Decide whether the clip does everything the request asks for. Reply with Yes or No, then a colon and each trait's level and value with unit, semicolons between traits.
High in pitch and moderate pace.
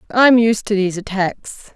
Yes: high, 210 Hz; average, 170 wpm